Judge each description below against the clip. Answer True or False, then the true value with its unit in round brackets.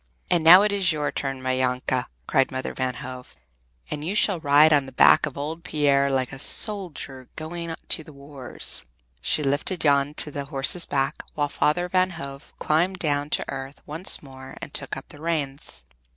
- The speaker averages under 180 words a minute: False (190 wpm)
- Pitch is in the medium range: True (145 Hz)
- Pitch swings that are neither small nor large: True (3.1 semitones)